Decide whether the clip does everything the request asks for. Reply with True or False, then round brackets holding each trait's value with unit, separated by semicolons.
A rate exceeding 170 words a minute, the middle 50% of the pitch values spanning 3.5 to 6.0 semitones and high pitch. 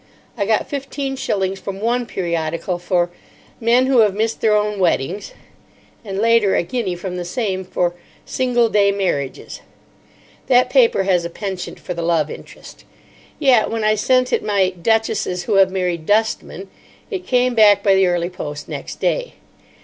False (165 wpm; 4.3 semitones; 200 Hz)